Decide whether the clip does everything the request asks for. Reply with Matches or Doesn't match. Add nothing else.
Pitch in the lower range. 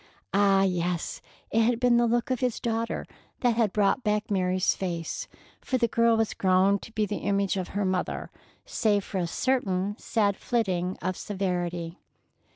Doesn't match